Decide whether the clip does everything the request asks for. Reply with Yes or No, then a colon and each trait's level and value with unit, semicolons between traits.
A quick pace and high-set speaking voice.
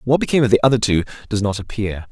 No: fast, 255 wpm; low, 115 Hz